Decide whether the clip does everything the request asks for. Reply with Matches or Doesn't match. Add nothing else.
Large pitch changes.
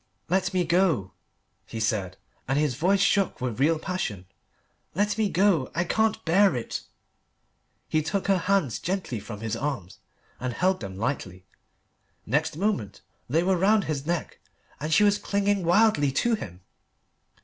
Matches